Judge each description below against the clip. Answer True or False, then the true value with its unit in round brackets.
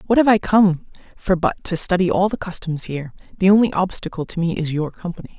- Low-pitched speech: False (185 Hz)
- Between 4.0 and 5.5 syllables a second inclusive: False (6.1 syllables/s)